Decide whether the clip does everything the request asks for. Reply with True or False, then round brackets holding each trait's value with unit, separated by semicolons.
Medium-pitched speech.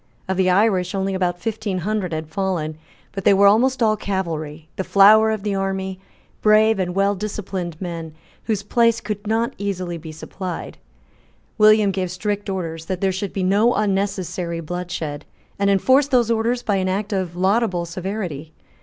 False (195 Hz)